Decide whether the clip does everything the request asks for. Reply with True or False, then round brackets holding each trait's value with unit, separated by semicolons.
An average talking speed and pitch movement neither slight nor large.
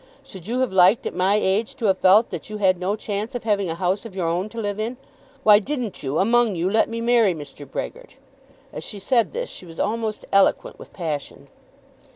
False (220 wpm; 3.7 semitones)